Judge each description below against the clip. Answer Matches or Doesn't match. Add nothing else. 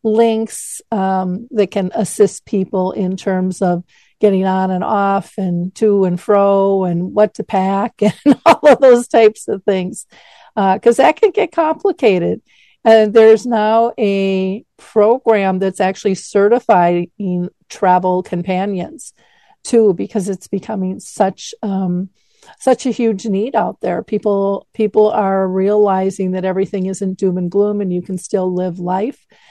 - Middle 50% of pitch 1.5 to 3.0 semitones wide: Matches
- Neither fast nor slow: Matches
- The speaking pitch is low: Doesn't match